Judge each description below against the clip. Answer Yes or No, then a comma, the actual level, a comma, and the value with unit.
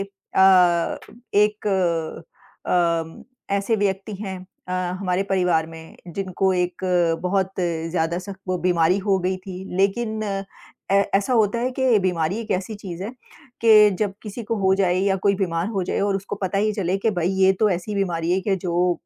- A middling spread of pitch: No, narrow, 2.2 semitones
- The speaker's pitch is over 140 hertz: Yes, high, 190 Hz